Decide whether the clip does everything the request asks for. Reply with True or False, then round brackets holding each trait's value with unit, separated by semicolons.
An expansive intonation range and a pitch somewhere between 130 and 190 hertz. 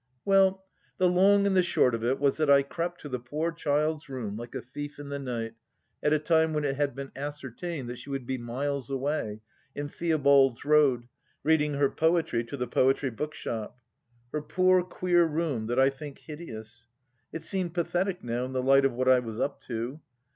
False (4.0 semitones; 140 Hz)